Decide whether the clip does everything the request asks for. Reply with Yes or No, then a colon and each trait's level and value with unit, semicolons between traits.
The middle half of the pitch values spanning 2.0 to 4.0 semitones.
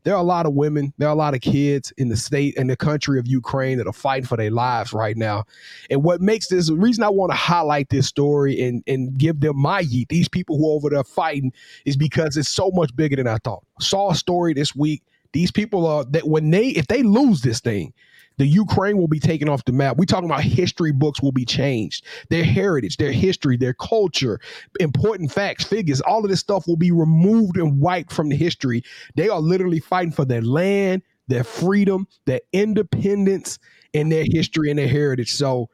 No: average, 5.1 semitones